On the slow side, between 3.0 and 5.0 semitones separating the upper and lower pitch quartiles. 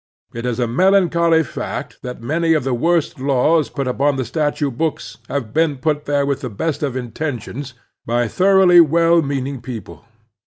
No: average, 170 wpm; average, 4.6 semitones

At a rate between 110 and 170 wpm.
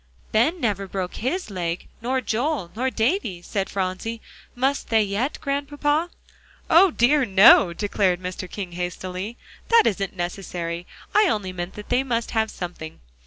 Yes: average, 145 wpm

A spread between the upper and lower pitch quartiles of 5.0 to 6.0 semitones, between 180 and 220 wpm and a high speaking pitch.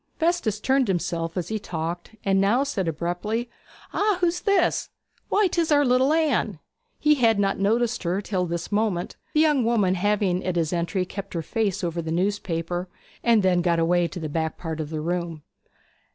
Yes: wide, 5.6 semitones; average, 185 wpm; high, 195 Hz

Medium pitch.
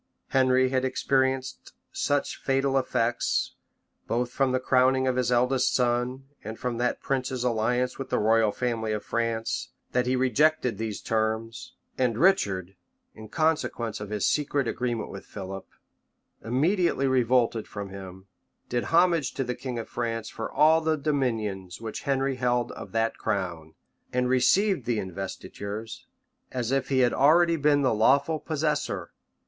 No: low, 125 Hz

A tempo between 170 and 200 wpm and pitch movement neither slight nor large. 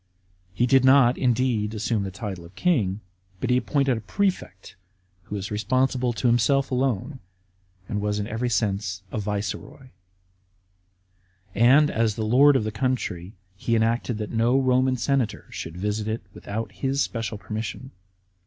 No: average, 155 wpm; average, 3.8 semitones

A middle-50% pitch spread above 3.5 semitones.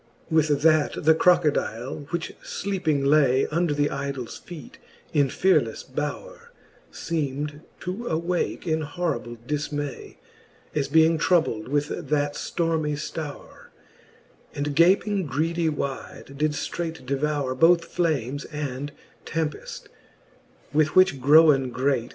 No: average, 2.9 semitones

